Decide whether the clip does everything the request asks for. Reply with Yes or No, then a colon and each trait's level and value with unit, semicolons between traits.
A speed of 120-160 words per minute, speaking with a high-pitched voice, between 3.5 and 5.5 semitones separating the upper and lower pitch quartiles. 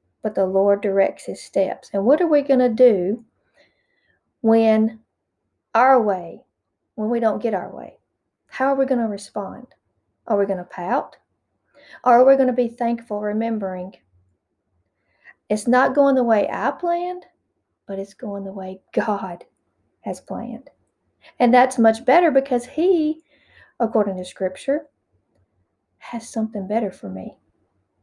Yes: average, 150 wpm; high, 225 Hz; average, 4.8 semitones